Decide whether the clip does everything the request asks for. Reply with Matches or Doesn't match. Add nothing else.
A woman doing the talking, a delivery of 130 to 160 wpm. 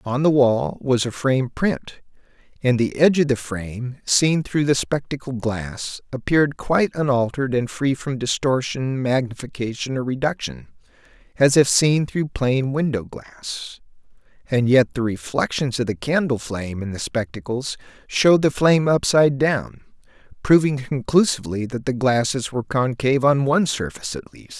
Doesn't match